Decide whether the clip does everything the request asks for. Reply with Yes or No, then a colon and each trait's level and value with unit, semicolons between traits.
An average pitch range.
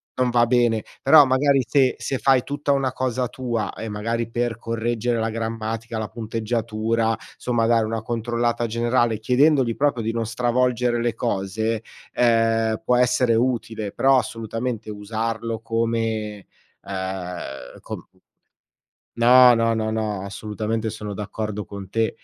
No: narrow, 1.8 semitones